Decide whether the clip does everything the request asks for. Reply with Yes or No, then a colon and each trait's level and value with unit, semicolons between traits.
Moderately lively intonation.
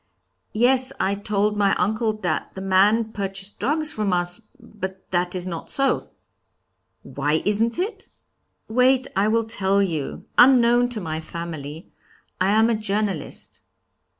Yes: average, 3.7 semitones